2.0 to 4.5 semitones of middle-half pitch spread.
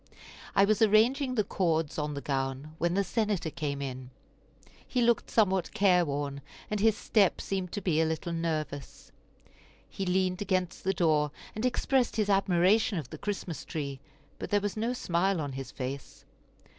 No: average, 5.3 semitones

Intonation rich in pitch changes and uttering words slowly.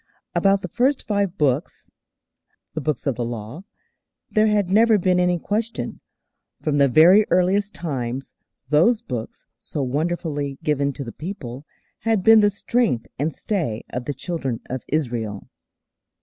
No: wide, 7.0 semitones; average, 150 wpm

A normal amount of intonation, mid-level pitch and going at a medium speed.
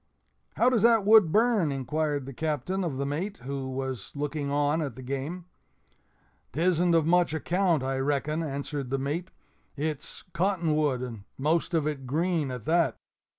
Yes: average, 4.0 semitones; medium, 150 Hz; average, 165 wpm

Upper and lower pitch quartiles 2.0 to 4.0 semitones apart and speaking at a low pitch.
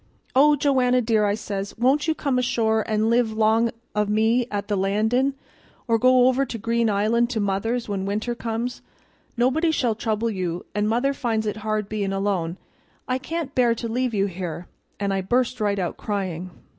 No: average, 3.5 semitones; high, 220 Hz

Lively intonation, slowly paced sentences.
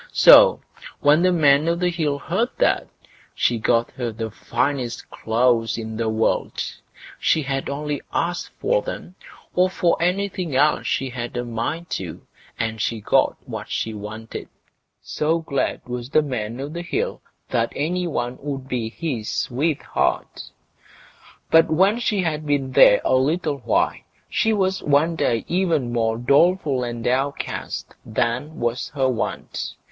No: wide, 5.8 semitones; average, 155 wpm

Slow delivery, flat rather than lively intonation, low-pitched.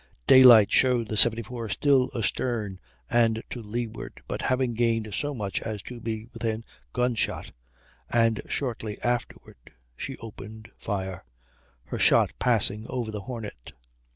Yes: slow, 130 wpm; narrow, 2.1 semitones; low, 115 Hz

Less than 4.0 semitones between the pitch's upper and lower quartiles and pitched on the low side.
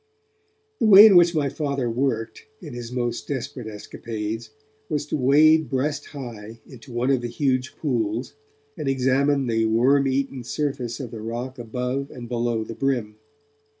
Yes: average, 3.1 semitones; low, 125 Hz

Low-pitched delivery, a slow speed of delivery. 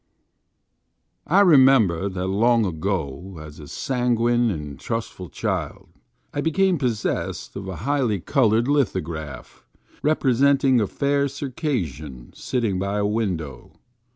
Yes: low, 110 Hz; slow, 110 wpm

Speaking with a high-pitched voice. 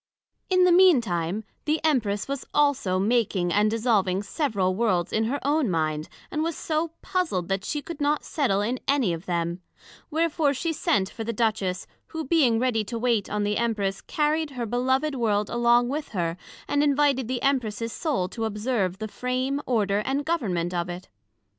Yes: high, 235 Hz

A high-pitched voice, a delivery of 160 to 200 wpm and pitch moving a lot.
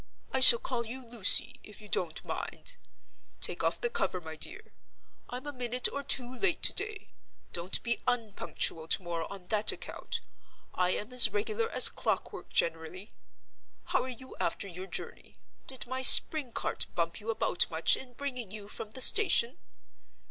Yes: high, 235 Hz; average, 170 wpm; wide, 5.9 semitones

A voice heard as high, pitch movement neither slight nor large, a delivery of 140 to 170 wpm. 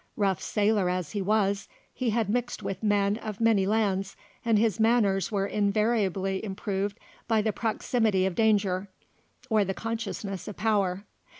No: high, 205 Hz; narrow, 2.2 semitones; average, 155 wpm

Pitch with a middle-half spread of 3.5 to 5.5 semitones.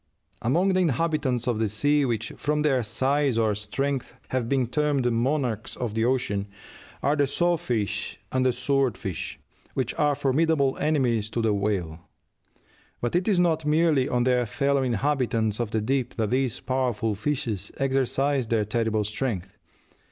Yes: average, 4.2 semitones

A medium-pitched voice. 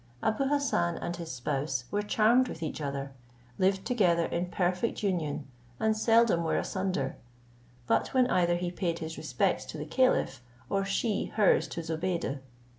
Yes: medium, 175 Hz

